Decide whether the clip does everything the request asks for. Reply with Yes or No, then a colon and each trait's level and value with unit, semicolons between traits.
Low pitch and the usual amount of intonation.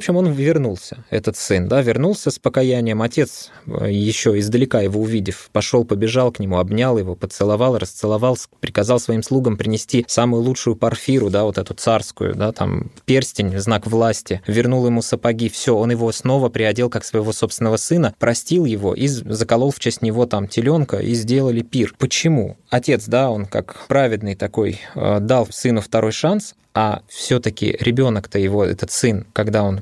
Yes: low, 115 Hz; average, 3.1 semitones